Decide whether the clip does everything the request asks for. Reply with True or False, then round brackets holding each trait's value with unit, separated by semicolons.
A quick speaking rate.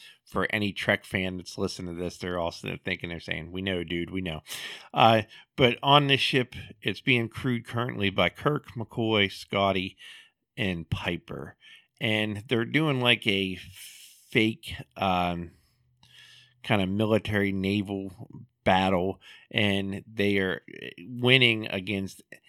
False (135 wpm)